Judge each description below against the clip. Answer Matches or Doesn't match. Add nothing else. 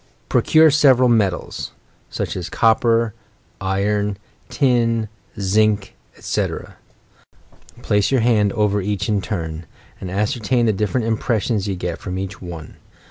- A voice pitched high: Doesn't match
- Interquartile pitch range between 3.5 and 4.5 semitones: Doesn't match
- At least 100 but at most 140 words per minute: Matches